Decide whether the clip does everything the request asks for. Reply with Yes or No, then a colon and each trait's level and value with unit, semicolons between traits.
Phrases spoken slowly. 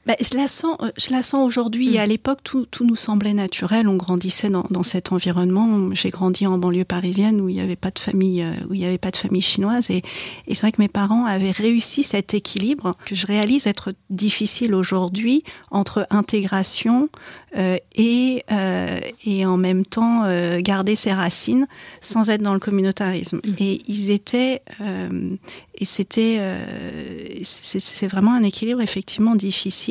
No: average, 185 wpm